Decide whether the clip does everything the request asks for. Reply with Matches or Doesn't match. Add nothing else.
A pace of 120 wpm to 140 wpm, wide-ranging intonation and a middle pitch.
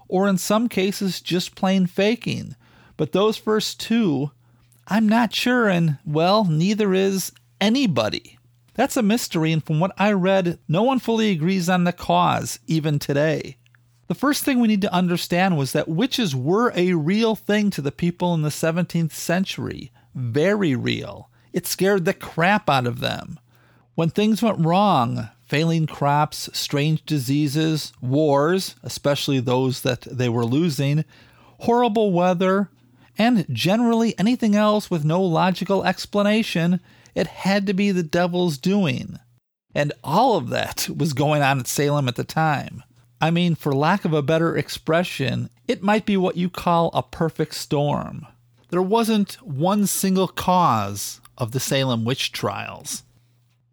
Doesn't match